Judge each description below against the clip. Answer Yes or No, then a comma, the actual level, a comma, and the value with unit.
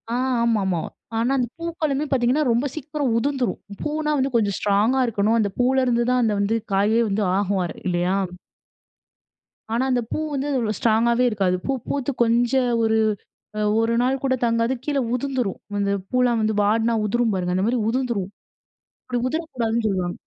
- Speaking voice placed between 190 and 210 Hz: No, high, 235 Hz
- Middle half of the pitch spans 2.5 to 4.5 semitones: Yes, average, 3.9 semitones